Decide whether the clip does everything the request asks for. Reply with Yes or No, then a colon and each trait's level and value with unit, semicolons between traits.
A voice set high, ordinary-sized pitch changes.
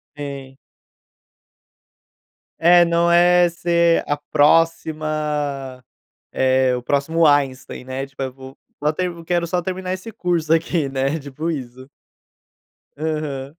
No: medium, 150 Hz; average, 3.9 semitones